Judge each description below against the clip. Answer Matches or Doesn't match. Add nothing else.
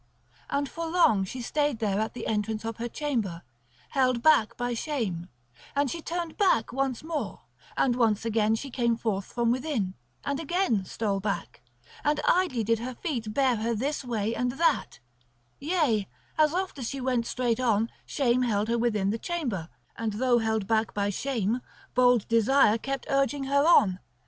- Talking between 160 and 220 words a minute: Matches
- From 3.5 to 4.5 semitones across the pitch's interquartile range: Matches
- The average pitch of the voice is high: Matches